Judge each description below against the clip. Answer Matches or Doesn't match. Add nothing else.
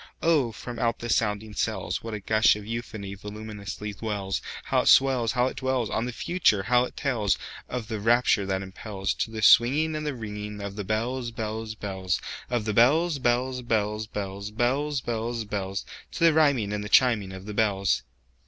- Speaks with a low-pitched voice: Matches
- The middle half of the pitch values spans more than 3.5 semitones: Doesn't match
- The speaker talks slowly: Doesn't match